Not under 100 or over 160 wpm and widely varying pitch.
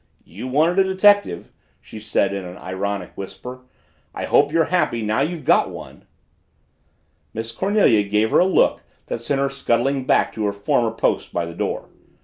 No: average, 175 wpm; wide, 7.0 semitones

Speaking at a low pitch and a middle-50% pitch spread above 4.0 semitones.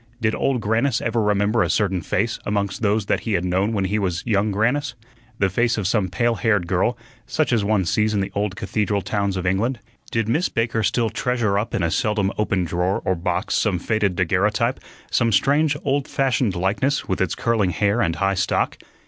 No: low, 105 Hz; average, 3.4 semitones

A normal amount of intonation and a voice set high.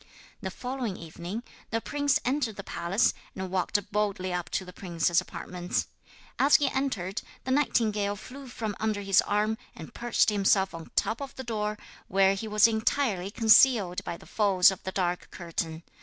Yes: average, 3.8 semitones; high, 205 Hz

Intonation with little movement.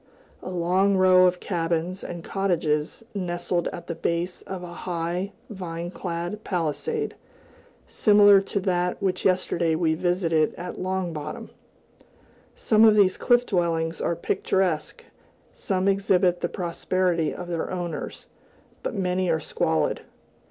Yes: narrow, 2.0 semitones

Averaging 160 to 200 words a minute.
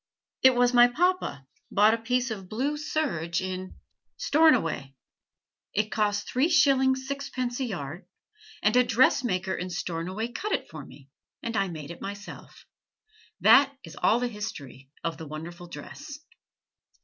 No: average, 150 wpm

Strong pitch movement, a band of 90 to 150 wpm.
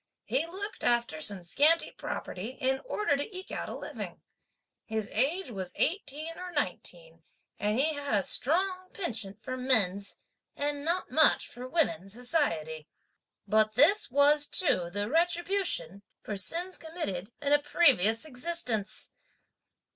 Yes: wide, 8.3 semitones; average, 140 wpm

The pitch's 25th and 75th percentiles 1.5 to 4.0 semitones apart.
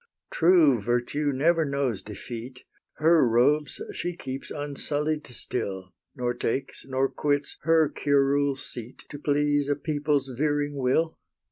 Yes: average, 2.8 semitones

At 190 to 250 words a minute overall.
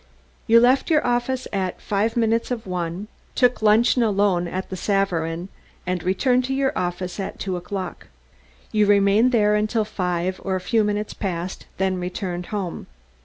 No: average, 165 wpm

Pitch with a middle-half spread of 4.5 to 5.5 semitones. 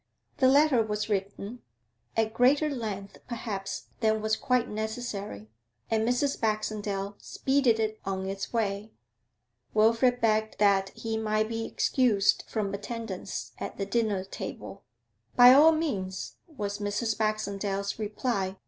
No: average, 2.9 semitones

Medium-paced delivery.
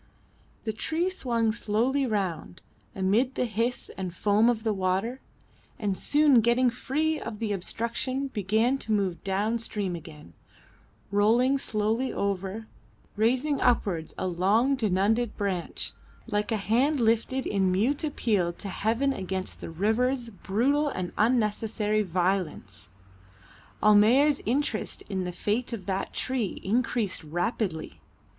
No: slow, 130 wpm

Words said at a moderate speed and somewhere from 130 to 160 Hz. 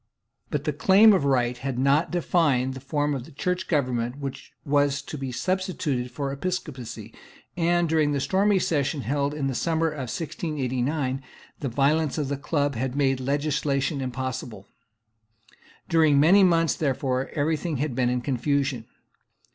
Yes: average, 155 wpm; medium, 140 Hz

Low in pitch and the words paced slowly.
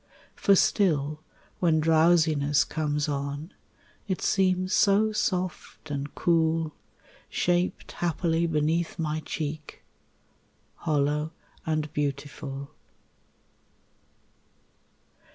No: medium, 155 Hz; slow, 80 wpm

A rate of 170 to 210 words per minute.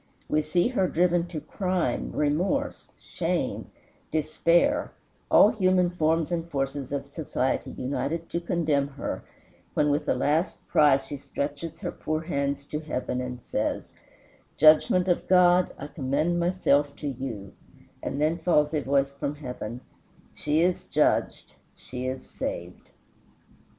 No: average, 140 wpm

